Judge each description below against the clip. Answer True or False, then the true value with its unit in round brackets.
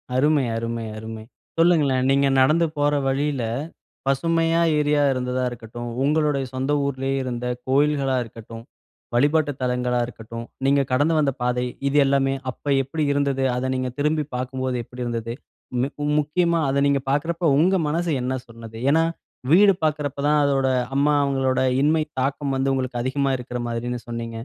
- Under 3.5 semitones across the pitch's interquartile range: True (3.0 semitones)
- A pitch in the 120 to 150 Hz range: True (135 Hz)